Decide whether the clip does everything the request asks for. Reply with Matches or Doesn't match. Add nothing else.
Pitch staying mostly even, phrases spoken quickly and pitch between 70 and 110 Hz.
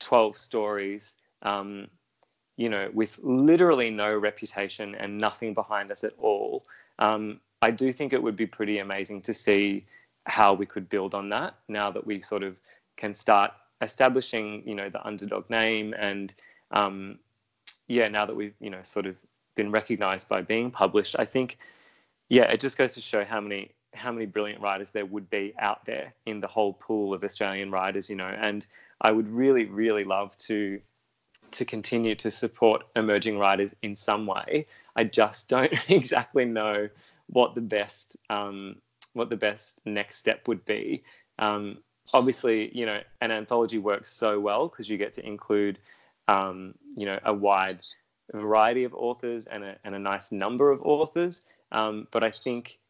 Doesn't match